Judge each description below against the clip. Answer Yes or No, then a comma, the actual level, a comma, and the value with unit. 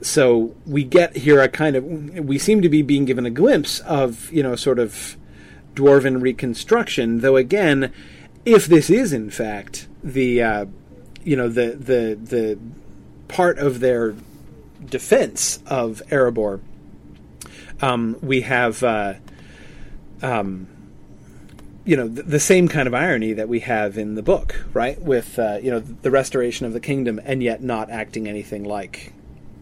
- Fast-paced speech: No, average, 155 wpm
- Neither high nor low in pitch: No, low, 125 Hz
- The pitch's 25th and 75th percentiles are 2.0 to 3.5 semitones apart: No, average, 4.3 semitones